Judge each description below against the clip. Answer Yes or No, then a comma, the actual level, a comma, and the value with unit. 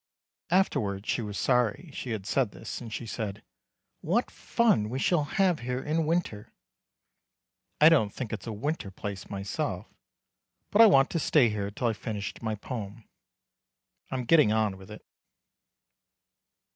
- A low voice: Yes, low, 115 Hz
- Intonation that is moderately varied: No, wide, 6.3 semitones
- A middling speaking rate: Yes, average, 155 wpm